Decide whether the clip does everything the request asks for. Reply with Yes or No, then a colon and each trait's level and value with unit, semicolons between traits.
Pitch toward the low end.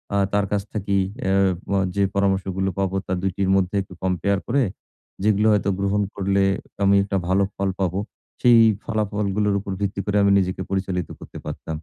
Yes: low, 100 Hz